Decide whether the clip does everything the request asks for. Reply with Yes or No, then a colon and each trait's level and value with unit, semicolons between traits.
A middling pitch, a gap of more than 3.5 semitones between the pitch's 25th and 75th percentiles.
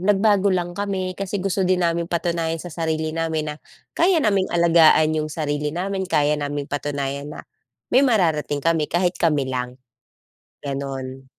Yes: medium, 165 Hz; average, 4.0 semitones